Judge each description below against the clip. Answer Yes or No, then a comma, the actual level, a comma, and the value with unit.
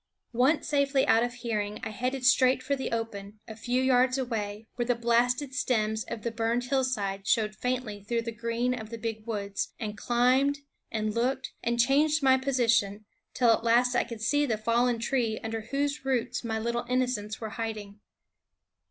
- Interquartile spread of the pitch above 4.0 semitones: No, narrow, 2.6 semitones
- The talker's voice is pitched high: Yes, high, 235 Hz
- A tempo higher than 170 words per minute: Yes, average, 180 wpm